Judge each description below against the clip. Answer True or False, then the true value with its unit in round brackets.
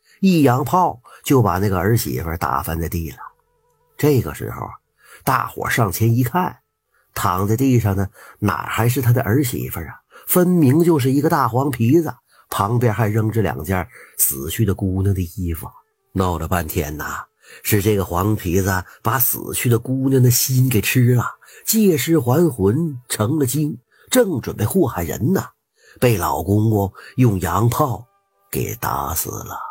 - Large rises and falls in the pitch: True (6.3 semitones)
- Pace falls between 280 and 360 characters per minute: False (225 characters per minute)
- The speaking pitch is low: True (120 Hz)